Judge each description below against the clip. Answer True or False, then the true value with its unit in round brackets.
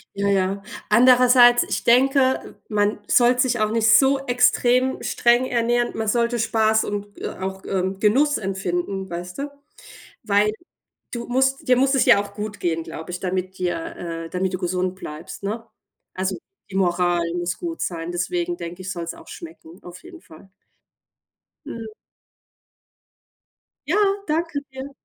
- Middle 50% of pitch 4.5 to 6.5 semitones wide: True (5.2 semitones)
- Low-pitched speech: False (210 Hz)